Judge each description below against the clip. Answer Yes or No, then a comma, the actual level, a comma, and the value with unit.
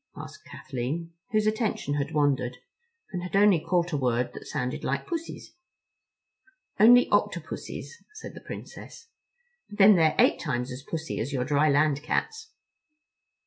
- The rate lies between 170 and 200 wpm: No, average, 145 wpm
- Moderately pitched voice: Yes, medium, 155 Hz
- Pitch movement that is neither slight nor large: No, wide, 7.1 semitones